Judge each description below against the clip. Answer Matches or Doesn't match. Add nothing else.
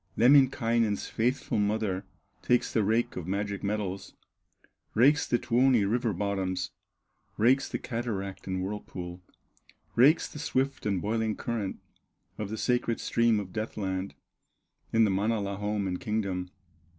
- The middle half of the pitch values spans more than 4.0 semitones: Doesn't match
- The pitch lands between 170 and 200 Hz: Doesn't match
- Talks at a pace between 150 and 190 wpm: Doesn't match